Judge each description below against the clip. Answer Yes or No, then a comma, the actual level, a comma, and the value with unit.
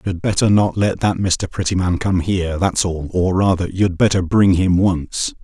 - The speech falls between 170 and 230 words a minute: Yes, average, 200 wpm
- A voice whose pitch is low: Yes, very low, 90 Hz